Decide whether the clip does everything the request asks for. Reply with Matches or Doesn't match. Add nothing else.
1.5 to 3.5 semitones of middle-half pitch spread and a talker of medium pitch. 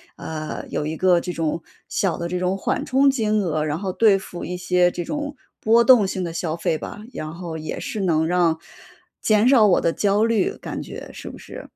Doesn't match